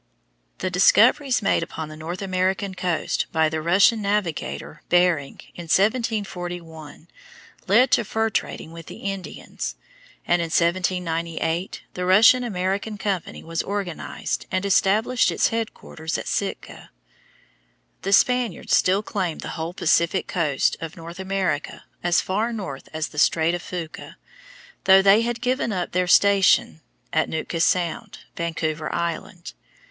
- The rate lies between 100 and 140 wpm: Yes, slow, 135 wpm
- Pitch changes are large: No, average, 3.4 semitones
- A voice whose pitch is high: No, medium, 180 Hz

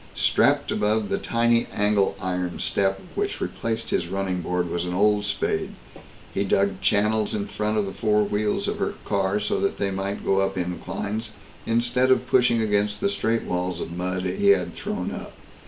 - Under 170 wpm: No, average, 185 wpm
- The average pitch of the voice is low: Yes, low, 100 Hz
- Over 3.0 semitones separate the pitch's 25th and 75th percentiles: No, narrow, 2.5 semitones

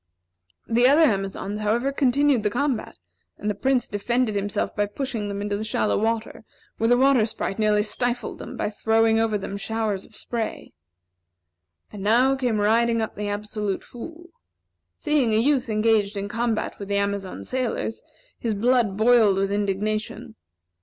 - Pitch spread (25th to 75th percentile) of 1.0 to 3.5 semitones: Yes, average, 2.9 semitones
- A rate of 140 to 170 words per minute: Yes, average, 160 wpm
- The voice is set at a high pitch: Yes, high, 220 Hz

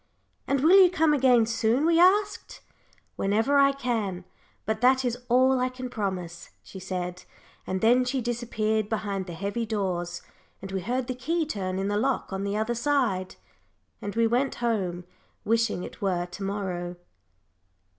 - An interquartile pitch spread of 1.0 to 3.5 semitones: No, average, 4.9 semitones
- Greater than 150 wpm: Yes, average, 165 wpm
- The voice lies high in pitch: Yes, high, 225 Hz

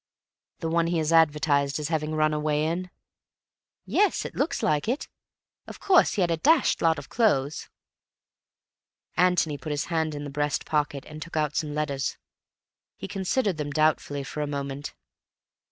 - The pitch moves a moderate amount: No, narrow, 2.3 semitones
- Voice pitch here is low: No, medium, 155 Hz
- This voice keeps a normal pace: Yes, average, 170 wpm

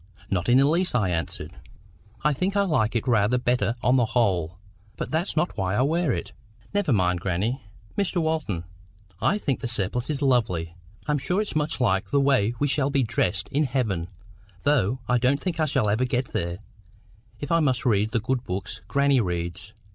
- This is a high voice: No, low, 125 Hz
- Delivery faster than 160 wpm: Yes, average, 195 wpm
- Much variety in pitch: Yes, wide, 6.3 semitones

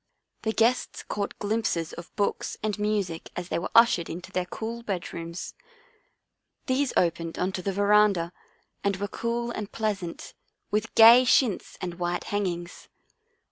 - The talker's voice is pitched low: No, high, 200 Hz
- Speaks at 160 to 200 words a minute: No, average, 145 wpm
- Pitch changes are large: No, average, 4.0 semitones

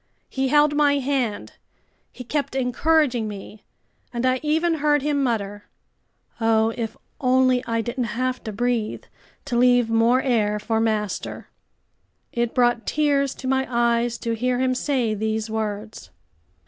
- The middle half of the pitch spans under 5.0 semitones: Yes, average, 2.9 semitones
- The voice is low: No, high, 245 Hz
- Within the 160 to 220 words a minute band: No, average, 145 wpm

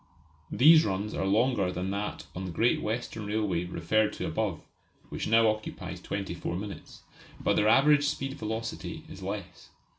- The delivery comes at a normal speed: Yes, average, 155 wpm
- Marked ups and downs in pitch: No, average, 3.2 semitones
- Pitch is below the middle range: Yes, low, 105 Hz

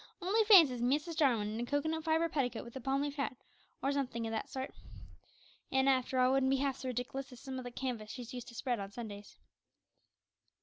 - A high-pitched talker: Yes, very high, 260 Hz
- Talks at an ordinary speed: No, fast, 220 wpm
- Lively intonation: No, average, 2.7 semitones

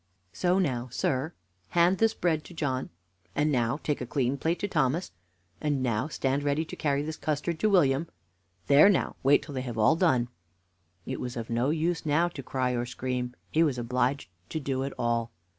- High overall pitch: No, medium, 140 Hz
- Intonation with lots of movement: No, average, 4.2 semitones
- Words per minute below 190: No, average, 195 wpm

